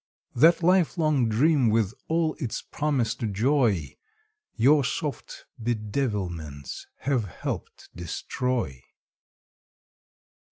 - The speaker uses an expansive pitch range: Yes, wide, 6.3 semitones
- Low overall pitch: Yes, low, 125 Hz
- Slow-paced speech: Yes, slow, 80 wpm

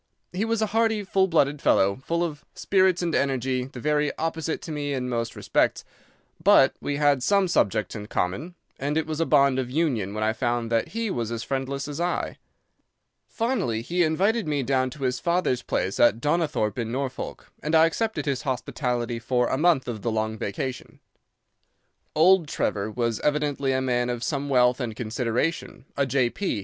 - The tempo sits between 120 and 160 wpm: No, average, 185 wpm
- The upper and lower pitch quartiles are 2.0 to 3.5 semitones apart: No, average, 5.2 semitones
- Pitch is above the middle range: No, low, 135 Hz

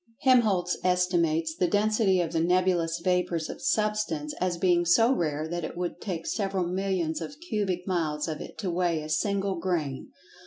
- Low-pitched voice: No, medium, 180 Hz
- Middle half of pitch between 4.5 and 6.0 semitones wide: No, average, 2.8 semitones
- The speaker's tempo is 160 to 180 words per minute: Yes, average, 170 wpm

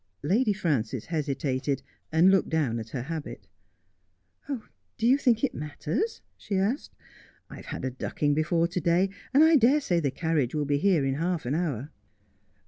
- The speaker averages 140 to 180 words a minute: No, average, 190 wpm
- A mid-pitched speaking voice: Yes, medium, 160 Hz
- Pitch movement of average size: No, wide, 5.9 semitones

